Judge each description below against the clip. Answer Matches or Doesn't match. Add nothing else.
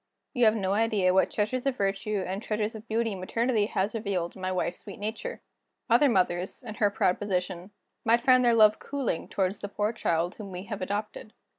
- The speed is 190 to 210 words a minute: Matches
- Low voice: Doesn't match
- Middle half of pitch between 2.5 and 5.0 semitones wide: Matches